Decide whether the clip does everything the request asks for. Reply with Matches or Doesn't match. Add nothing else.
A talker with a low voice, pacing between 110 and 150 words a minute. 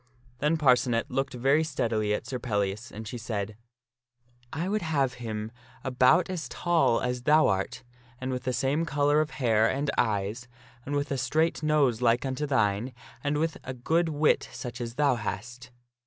Doesn't match